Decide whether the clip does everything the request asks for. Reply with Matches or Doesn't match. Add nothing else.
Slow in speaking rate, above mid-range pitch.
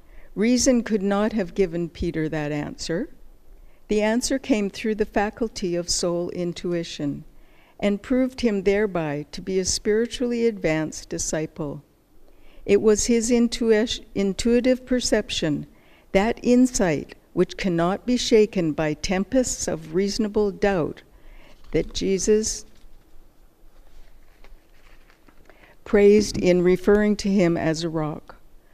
Matches